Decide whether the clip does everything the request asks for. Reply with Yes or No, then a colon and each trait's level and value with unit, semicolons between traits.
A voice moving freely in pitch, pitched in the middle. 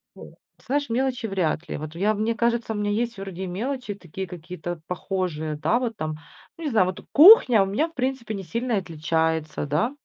No: wide, 5.8 semitones; high, 200 Hz